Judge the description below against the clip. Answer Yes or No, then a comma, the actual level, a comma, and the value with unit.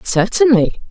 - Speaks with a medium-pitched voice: No, high, 230 Hz